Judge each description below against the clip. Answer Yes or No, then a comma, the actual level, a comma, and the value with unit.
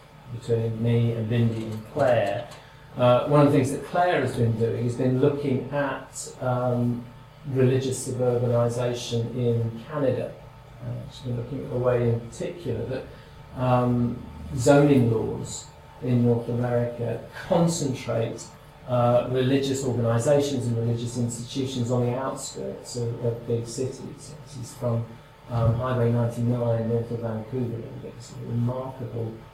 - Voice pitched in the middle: No, low, 125 Hz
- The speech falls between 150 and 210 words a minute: No, average, 140 wpm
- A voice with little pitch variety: Yes, narrow, 2.1 semitones